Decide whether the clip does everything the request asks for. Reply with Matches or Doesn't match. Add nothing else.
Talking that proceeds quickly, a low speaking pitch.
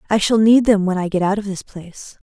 Doesn't match